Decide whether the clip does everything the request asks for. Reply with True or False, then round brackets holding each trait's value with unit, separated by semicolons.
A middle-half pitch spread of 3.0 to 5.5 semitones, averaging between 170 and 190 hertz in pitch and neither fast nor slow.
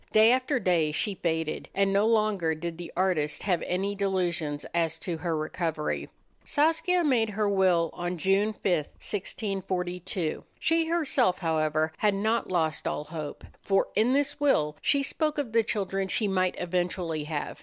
True (4.7 semitones; 185 Hz; 160 wpm)